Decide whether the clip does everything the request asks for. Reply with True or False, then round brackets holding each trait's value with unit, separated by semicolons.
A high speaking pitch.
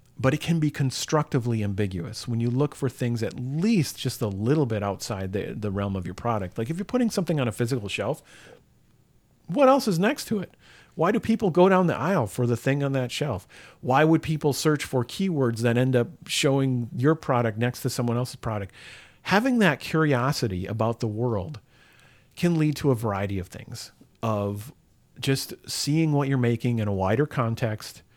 False (125 Hz)